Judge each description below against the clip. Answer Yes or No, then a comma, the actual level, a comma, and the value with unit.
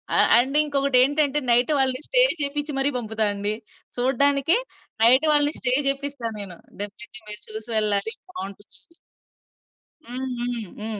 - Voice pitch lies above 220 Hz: Yes, very high, 255 Hz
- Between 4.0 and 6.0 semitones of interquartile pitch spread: Yes, average, 4.4 semitones